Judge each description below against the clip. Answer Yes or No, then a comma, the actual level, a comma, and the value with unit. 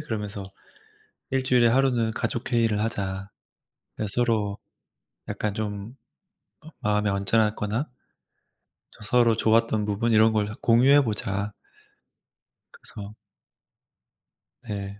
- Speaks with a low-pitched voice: Yes, low, 110 Hz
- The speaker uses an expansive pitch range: No, narrow, 2.3 semitones